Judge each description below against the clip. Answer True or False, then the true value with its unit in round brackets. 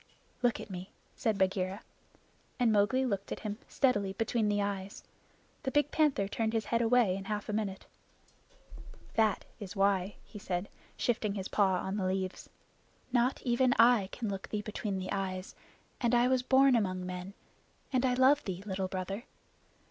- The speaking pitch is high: True (205 Hz)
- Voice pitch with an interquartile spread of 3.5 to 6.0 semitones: True (3.9 semitones)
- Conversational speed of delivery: True (170 wpm)